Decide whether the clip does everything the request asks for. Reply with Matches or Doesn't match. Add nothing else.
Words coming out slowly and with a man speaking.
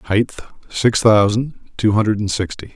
Matches